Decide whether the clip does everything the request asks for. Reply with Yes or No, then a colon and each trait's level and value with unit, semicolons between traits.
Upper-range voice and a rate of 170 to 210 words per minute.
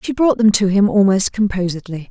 Yes: high, 200 Hz; average, 200 wpm